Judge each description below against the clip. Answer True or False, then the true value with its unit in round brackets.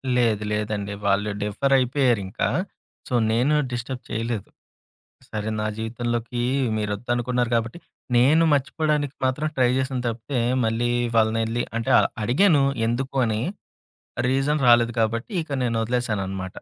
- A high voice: False (120 Hz)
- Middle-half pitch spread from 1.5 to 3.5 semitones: True (2.9 semitones)